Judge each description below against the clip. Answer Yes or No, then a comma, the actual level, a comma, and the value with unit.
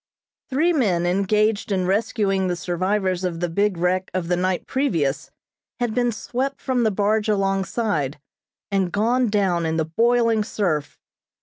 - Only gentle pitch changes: No, average, 3.9 semitones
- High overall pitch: Yes, high, 195 Hz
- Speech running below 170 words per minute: Yes, average, 150 wpm